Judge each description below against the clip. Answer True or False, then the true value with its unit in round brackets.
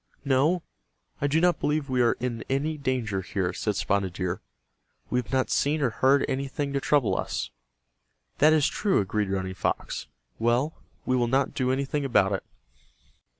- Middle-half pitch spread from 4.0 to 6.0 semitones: True (5.0 semitones)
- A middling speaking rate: True (170 wpm)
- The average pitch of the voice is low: True (130 Hz)